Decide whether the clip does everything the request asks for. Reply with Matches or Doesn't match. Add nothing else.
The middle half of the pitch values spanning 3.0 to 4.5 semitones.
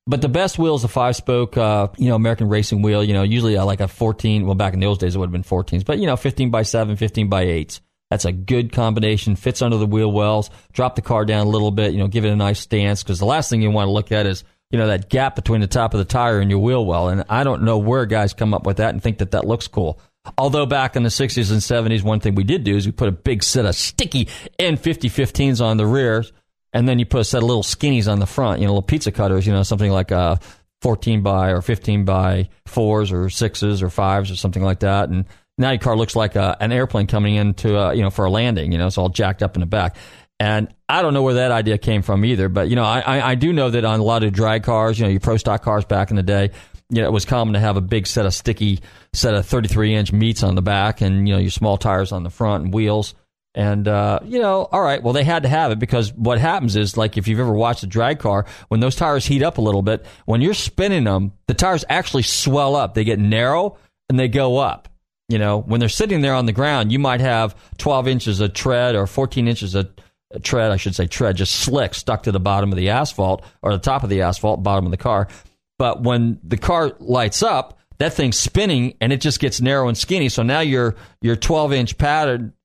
Matches